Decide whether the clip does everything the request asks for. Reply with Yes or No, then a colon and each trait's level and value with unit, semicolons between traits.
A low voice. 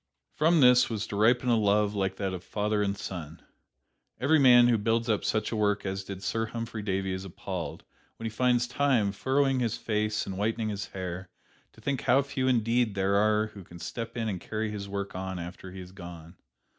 Yes: low, 105 Hz